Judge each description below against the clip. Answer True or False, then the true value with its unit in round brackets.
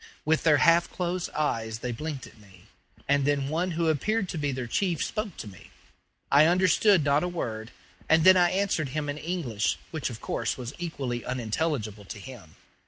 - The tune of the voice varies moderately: False (6.1 semitones)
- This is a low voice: False (150 Hz)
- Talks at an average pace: True (190 wpm)